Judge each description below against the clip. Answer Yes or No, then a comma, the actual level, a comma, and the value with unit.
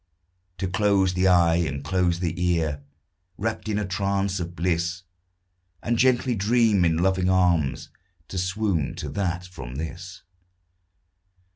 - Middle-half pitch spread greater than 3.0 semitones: No, narrow, 2.6 semitones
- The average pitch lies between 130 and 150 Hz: No, very low, 90 Hz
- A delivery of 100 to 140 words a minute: Yes, slow, 135 wpm